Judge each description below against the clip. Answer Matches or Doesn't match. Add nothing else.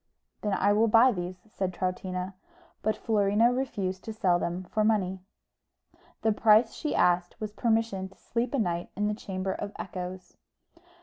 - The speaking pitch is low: Doesn't match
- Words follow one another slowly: Doesn't match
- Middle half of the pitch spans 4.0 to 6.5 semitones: Doesn't match